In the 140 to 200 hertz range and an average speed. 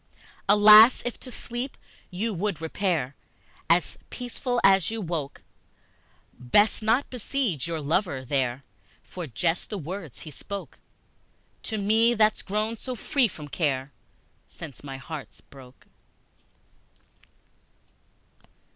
No: high, 190 Hz; slow, 115 wpm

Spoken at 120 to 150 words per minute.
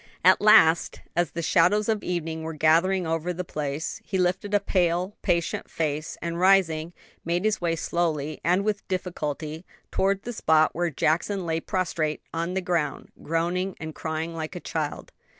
No: average, 170 wpm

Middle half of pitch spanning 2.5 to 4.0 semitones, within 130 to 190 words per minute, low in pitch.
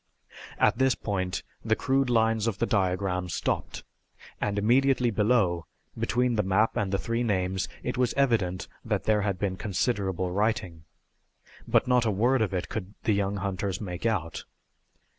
Yes: average, 3.7 semitones; average, 160 wpm; low, 105 Hz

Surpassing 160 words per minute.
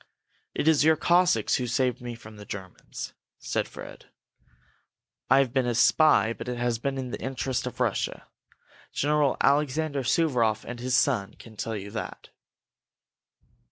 No: average, 155 wpm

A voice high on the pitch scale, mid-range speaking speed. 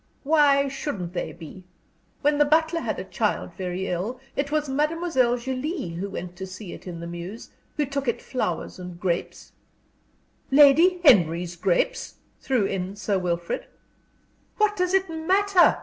Yes: very high, 255 Hz; average, 160 wpm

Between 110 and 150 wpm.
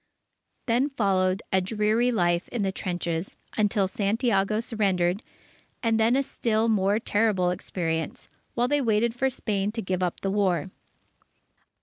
Yes: average, 140 wpm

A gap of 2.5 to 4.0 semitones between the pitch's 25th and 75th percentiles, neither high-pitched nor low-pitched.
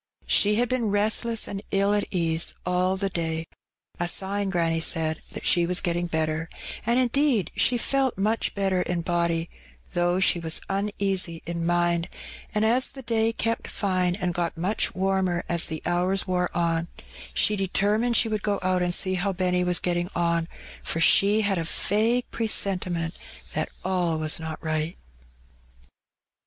Yes: average, 3.1 semitones; medium, 180 Hz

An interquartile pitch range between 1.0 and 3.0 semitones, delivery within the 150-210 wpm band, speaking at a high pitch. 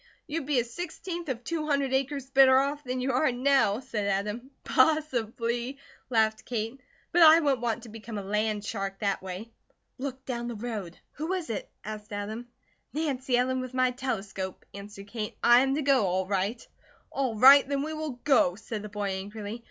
No: average, 4.4 semitones; average, 190 wpm; high, 245 Hz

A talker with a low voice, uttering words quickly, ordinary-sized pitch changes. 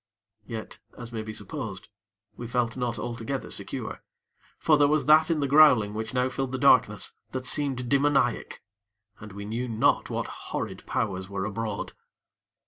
No: low, 120 Hz; average, 160 wpm; average, 3.9 semitones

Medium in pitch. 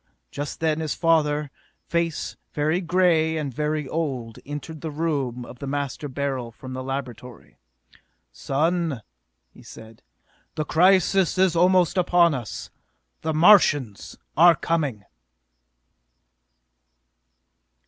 Yes: medium, 150 Hz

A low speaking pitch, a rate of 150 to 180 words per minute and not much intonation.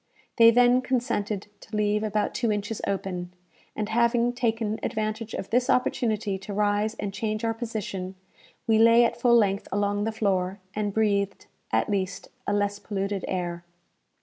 No: high, 210 Hz; average, 160 wpm; narrow, 2.3 semitones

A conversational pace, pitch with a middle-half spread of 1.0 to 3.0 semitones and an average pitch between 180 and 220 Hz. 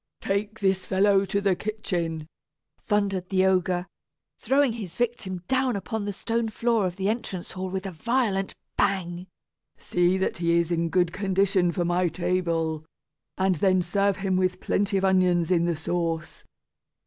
Yes: average, 160 wpm; narrow, 2.4 semitones; high, 190 Hz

